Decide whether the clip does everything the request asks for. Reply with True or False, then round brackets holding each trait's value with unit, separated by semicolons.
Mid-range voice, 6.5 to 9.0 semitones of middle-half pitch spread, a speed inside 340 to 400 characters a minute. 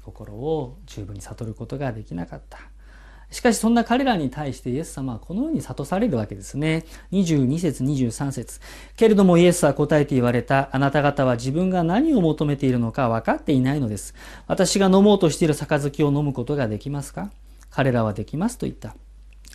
False (145 Hz; 5.7 semitones; 380 characters per minute)